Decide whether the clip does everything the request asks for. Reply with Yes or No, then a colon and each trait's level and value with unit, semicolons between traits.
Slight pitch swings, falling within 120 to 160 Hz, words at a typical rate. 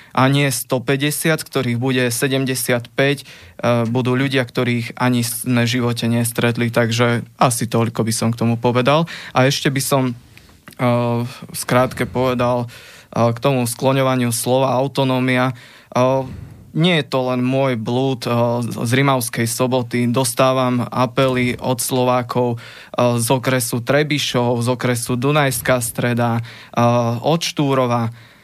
Yes: narrow, 1.9 semitones; low, 125 Hz; average, 130 wpm